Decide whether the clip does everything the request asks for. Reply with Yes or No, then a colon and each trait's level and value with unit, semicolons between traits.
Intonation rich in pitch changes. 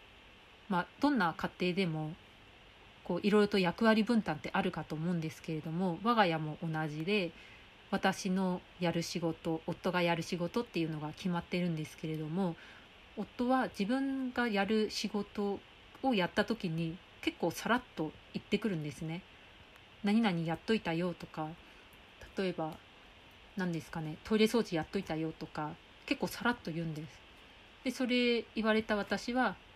No: average, 4.8 semitones